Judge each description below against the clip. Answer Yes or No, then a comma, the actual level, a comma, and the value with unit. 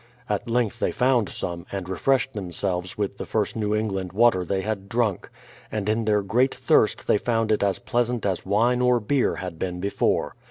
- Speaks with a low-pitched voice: Yes, low, 105 Hz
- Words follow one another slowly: No, average, 200 wpm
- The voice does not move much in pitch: No, average, 3.6 semitones